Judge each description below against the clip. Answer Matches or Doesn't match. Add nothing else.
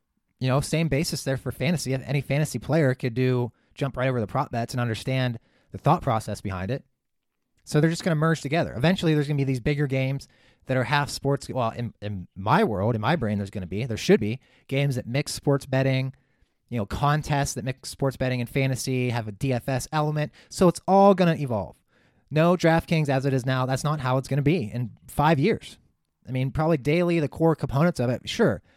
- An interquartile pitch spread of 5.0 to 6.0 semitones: Doesn't match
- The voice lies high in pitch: Doesn't match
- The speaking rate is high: Matches